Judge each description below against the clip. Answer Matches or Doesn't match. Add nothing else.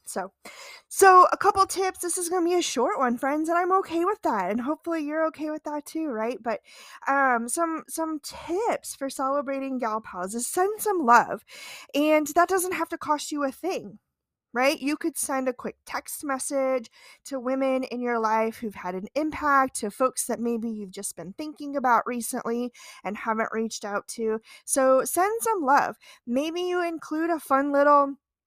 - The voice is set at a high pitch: Matches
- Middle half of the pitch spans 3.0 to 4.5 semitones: Doesn't match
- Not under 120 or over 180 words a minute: Doesn't match